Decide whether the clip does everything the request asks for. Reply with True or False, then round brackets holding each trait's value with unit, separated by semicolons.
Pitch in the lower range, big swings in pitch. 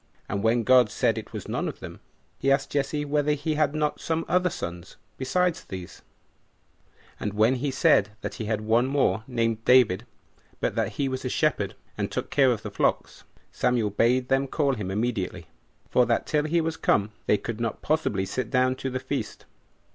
False (125 Hz; 4.7 semitones)